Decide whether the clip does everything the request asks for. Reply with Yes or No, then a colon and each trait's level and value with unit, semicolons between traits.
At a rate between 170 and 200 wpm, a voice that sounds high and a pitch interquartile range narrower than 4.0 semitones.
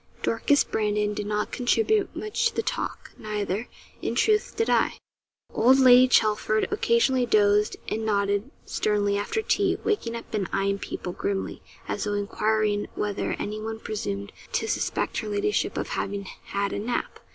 No: average, 155 wpm; high, 215 Hz; average, 3.3 semitones